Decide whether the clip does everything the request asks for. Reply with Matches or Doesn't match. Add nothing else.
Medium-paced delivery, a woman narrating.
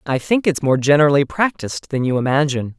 Doesn't match